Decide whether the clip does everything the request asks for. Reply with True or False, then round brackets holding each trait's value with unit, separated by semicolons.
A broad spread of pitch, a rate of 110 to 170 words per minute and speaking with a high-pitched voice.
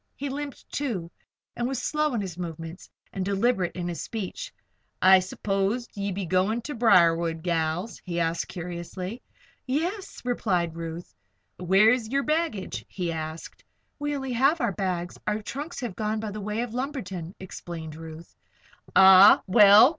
True (5.8 semitones; 155 wpm; 195 Hz)